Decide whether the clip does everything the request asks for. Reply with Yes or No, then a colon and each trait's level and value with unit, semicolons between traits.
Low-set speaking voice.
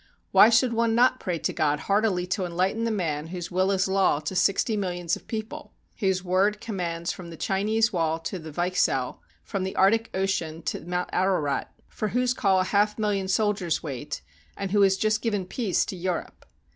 No: high, 190 Hz